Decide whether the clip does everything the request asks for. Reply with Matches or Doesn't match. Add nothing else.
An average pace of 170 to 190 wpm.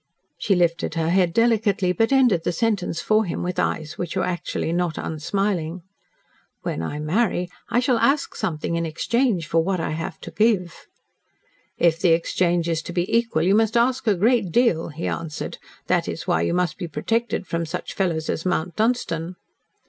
Matches